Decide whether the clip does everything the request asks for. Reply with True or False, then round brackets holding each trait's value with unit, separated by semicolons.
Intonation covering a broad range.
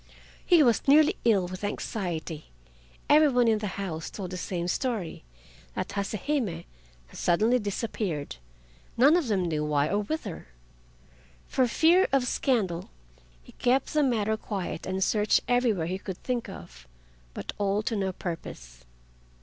True (6.0 semitones)